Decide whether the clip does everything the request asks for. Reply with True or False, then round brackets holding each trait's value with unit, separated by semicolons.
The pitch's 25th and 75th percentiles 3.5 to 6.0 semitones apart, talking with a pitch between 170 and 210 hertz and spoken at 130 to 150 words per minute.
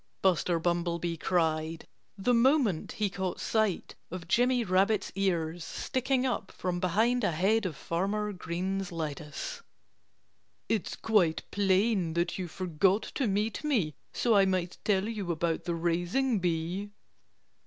True (3.9 semitones; 185 Hz; 135 wpm)